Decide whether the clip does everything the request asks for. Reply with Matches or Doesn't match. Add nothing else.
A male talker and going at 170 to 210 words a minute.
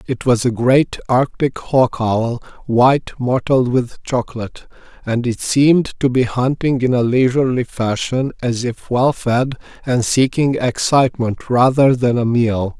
Doesn't match